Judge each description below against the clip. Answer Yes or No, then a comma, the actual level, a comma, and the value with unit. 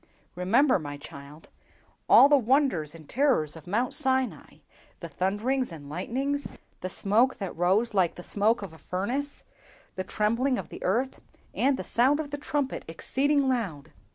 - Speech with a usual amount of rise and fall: No, wide, 7.0 semitones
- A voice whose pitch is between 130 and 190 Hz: No, high, 225 Hz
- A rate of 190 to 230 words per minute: No, average, 155 wpm